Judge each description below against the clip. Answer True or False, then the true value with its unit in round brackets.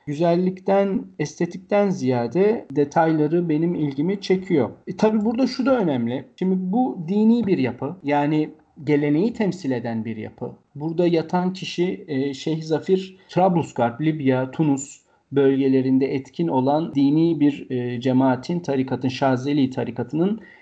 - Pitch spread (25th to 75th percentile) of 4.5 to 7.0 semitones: True (5.3 semitones)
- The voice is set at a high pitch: False (155 Hz)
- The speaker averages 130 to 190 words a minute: False (120 wpm)